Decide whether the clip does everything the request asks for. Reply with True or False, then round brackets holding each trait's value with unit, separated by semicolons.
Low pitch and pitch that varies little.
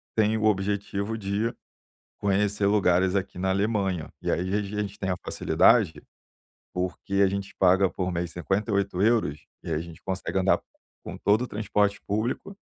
True (100 Hz; 2.0 semitones)